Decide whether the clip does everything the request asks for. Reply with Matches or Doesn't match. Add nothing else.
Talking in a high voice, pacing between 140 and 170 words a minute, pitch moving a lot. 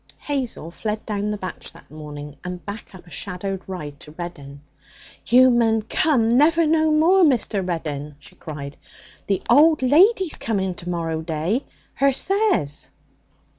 Matches